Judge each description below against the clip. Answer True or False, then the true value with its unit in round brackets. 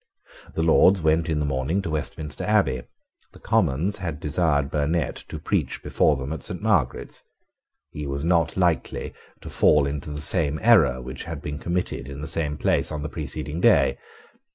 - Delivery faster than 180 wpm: False (175 wpm)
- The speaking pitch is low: True (75 Hz)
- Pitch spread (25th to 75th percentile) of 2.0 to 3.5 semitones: True (2.8 semitones)